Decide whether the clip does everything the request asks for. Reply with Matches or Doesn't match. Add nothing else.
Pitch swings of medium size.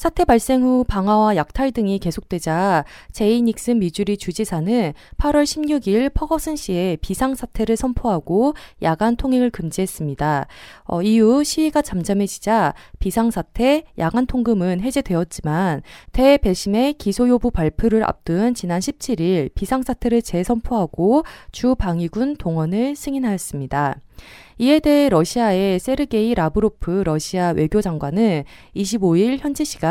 Doesn't match